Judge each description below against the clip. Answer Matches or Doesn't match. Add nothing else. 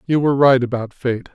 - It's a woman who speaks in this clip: Doesn't match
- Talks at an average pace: Doesn't match